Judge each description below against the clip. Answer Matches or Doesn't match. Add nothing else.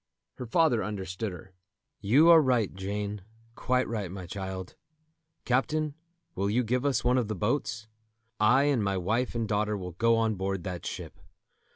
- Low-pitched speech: Matches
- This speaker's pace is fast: Doesn't match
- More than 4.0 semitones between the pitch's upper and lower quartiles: Matches